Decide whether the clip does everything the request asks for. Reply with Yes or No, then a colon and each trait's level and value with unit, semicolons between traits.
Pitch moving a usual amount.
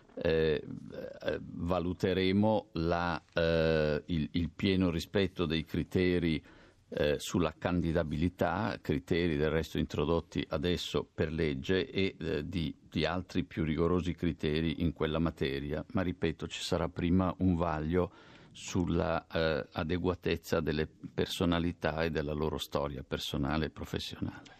No: narrow, 2.2 semitones